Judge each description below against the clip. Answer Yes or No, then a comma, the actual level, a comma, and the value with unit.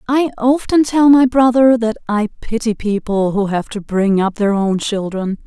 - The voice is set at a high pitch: Yes, high, 225 Hz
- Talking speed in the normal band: Yes, average, 185 wpm